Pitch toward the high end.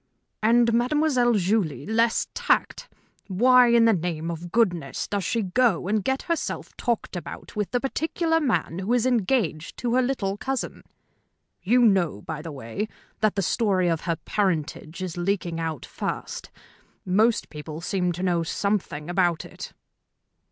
Yes: high, 200 Hz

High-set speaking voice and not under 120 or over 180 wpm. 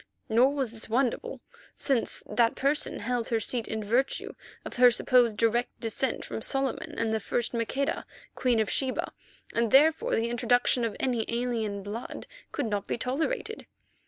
Yes: high, 240 Hz; average, 160 wpm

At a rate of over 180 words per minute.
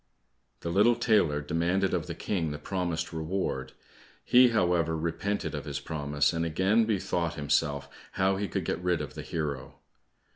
No: average, 160 wpm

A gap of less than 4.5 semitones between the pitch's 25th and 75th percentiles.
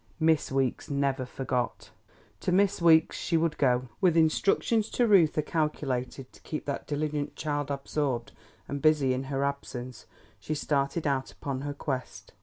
Yes: average, 2.9 semitones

